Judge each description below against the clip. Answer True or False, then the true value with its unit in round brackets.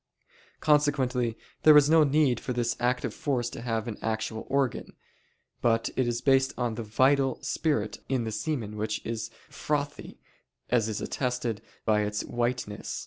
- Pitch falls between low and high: False (120 Hz)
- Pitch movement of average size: True (3.4 semitones)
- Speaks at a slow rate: False (155 wpm)